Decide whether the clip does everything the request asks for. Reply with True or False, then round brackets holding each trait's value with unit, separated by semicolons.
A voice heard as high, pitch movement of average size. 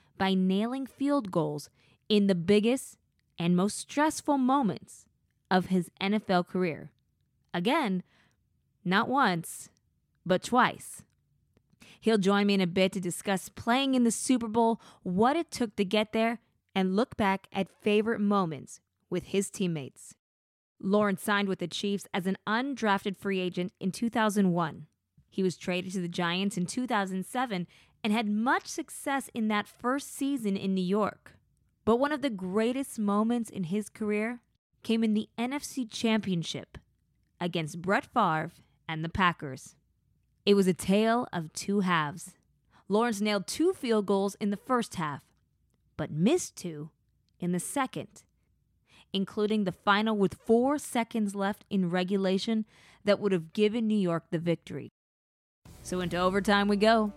True (200 Hz; 3.8 semitones)